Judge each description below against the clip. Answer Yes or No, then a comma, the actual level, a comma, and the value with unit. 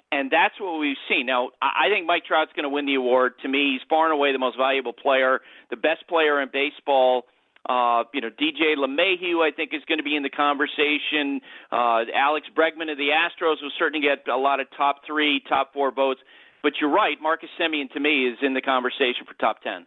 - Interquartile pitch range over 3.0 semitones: No, average, 2.7 semitones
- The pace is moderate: No, fast, 225 wpm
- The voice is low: No, medium, 145 Hz